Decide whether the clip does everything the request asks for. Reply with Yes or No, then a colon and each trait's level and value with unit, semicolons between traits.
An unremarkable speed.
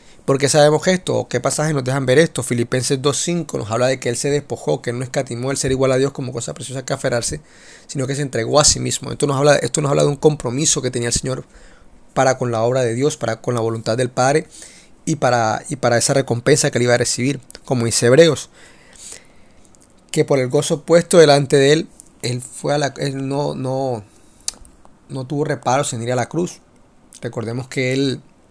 No: fast, 220 wpm